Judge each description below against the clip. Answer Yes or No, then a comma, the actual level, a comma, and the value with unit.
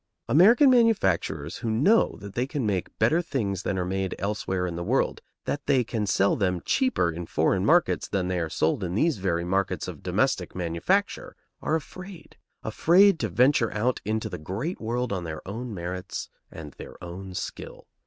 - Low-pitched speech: Yes, low, 100 Hz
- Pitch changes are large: Yes, wide, 7.2 semitones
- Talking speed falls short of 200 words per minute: Yes, average, 185 wpm